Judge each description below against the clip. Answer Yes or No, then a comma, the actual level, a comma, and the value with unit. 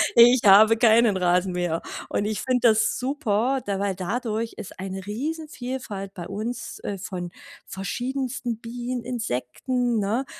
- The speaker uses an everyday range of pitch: Yes, average, 4.1 semitones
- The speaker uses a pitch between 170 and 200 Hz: No, high, 220 Hz